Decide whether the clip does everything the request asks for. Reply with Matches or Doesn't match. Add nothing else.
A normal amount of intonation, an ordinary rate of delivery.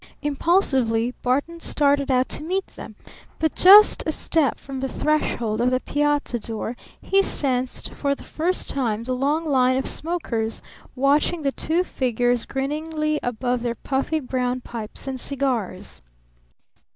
Matches